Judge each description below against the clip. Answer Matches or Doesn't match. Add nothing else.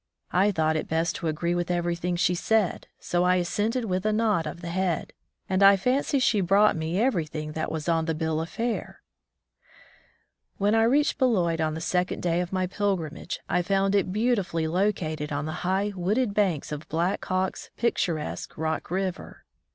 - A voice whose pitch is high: Doesn't match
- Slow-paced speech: Doesn't match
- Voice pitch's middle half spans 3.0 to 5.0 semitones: Matches